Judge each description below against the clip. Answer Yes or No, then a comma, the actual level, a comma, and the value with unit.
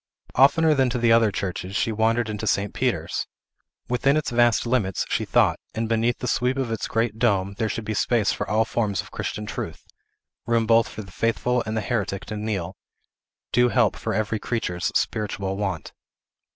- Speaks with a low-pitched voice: Yes, low, 110 Hz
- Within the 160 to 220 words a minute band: Yes, average, 190 wpm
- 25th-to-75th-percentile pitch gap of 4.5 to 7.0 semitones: No, narrow, 2.5 semitones